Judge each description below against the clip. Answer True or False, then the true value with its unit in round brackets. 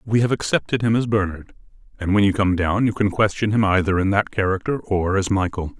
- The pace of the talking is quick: True (230 wpm)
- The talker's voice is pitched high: False (100 Hz)